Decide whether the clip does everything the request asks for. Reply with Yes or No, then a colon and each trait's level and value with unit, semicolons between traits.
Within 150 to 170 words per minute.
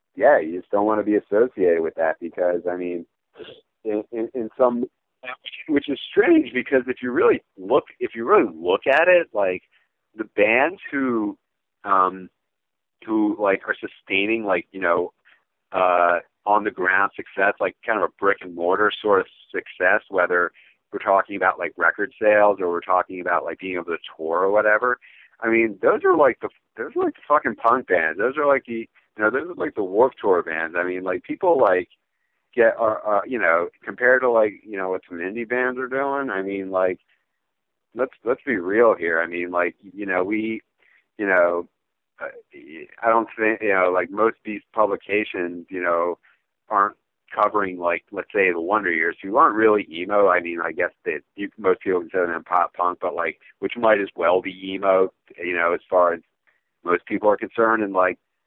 No: average, 200 wpm